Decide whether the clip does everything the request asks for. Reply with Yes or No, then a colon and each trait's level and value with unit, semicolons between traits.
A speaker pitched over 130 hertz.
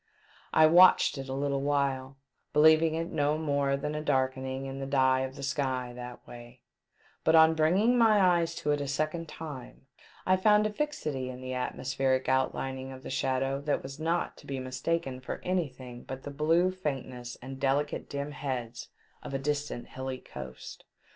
Yes: medium, 140 Hz